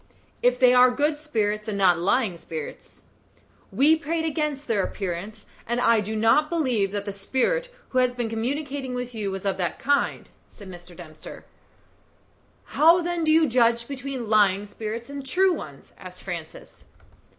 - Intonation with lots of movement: Yes, wide, 5.7 semitones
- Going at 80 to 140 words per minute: No, average, 165 wpm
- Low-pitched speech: No, high, 245 Hz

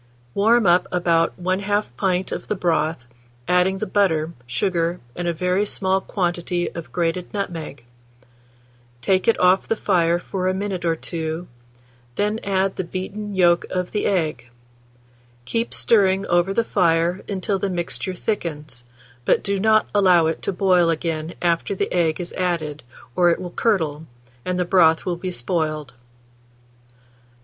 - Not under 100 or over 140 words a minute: No, average, 155 wpm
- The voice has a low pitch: No, medium, 180 Hz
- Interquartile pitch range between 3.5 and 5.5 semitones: No, narrow, 2.5 semitones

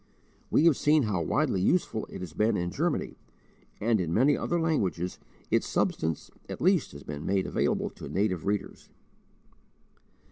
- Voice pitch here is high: No, low, 100 Hz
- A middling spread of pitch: No, wide, 8.6 semitones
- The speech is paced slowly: No, average, 155 wpm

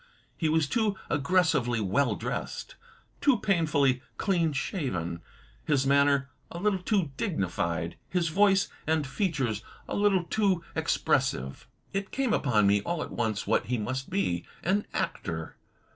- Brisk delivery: No, average, 145 wpm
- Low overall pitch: No, medium, 150 Hz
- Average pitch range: No, wide, 7.9 semitones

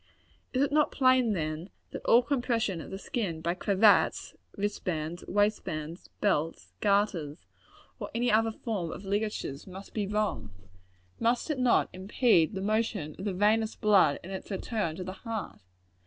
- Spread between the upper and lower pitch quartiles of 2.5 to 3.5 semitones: No, average, 4.2 semitones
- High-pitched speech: Yes, high, 205 Hz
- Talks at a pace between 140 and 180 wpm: Yes, average, 155 wpm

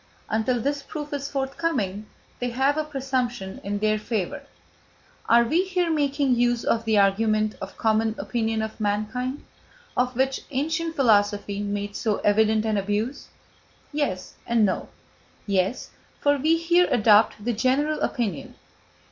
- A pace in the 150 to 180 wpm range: No, average, 140 wpm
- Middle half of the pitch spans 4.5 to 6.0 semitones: Yes, average, 4.8 semitones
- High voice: Yes, high, 235 Hz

